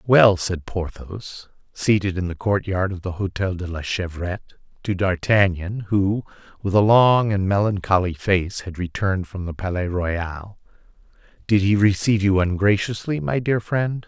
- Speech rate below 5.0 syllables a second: Yes, 4.5 syllables/s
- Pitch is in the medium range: No, very low, 95 Hz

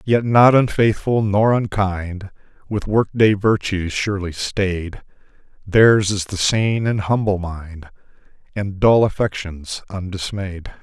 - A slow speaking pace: Yes, slow, 120 wpm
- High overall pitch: No, low, 100 Hz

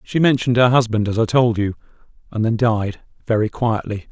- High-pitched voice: No, low, 115 Hz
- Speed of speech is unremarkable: Yes, average, 190 wpm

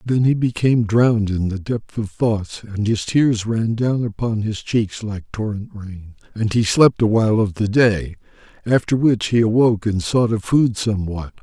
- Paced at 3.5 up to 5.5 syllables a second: Yes, 4.6 syllables/s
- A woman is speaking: No, male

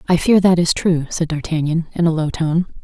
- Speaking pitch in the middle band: Yes, medium, 165 Hz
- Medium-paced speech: No, fast, 235 wpm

